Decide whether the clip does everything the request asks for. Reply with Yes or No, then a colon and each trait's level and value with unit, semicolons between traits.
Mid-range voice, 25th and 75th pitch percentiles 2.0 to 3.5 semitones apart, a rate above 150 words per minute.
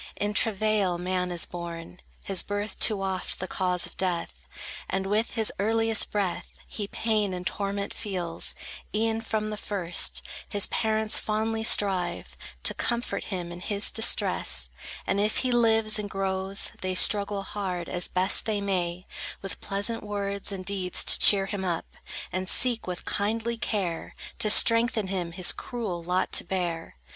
No: high, 200 Hz; average, 2.8 semitones; average, 160 wpm